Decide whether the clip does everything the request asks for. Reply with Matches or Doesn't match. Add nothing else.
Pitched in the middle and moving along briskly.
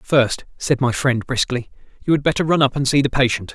Doesn't match